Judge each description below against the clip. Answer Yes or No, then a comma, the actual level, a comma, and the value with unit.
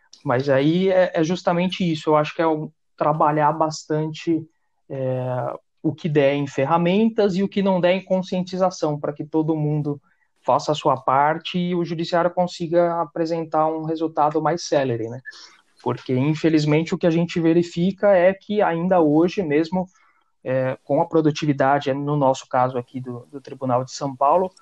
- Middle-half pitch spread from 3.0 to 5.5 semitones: Yes, average, 3.5 semitones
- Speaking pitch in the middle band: Yes, medium, 160 Hz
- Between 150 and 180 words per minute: Yes, average, 170 wpm